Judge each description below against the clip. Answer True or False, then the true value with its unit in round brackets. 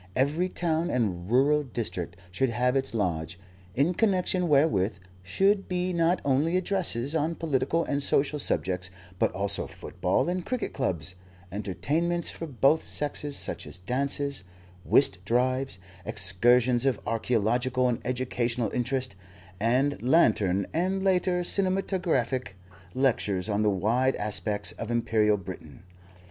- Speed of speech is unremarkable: False (130 wpm)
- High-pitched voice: False (130 Hz)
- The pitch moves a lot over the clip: True (7.1 semitones)